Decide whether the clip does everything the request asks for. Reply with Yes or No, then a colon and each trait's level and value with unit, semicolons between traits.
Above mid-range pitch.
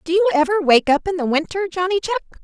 Yes: very high, 340 Hz